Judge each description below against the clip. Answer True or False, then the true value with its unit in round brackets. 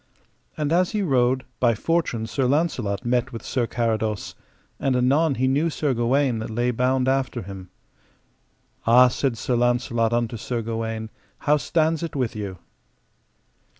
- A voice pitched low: True (125 Hz)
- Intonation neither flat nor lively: True (3.2 semitones)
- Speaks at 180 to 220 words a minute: False (150 wpm)